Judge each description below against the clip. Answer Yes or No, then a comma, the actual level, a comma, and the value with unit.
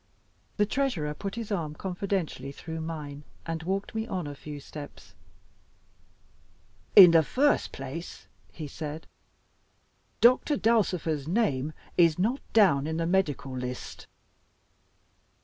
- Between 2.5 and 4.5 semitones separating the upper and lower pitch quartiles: No, average, 5.1 semitones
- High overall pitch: No, medium, 165 Hz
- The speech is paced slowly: Yes, slow, 120 wpm